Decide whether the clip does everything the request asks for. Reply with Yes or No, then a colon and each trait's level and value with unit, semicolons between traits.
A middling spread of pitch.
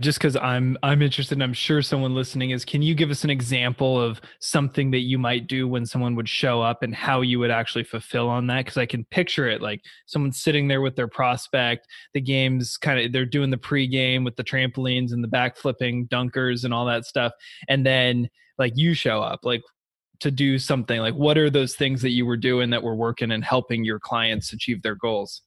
No: narrow, 2.3 semitones